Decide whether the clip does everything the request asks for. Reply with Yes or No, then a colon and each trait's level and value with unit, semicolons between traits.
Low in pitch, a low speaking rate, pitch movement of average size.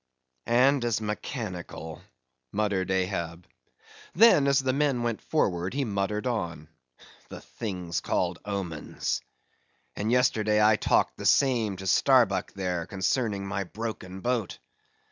Yes: low, 105 Hz; slow, 125 wpm; average, 4.5 semitones